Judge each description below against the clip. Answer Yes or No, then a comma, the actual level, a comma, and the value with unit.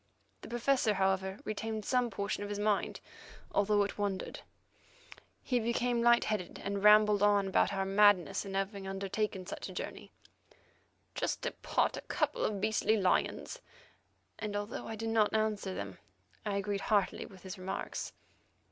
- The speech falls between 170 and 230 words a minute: No, average, 155 wpm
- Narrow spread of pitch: Yes, narrow, 1.9 semitones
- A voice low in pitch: No, high, 205 Hz